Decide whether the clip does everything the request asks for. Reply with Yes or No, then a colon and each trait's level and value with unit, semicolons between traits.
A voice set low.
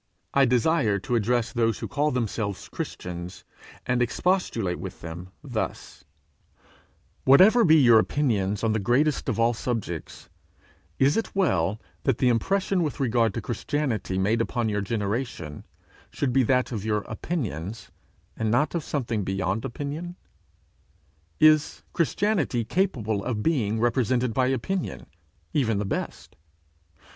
Yes: low, 120 Hz